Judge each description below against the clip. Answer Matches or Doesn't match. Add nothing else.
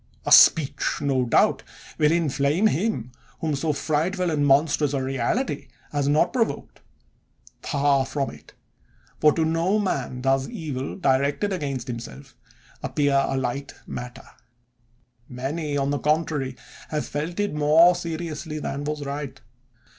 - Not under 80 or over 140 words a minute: Matches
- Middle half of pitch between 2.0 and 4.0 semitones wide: Matches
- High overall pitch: Doesn't match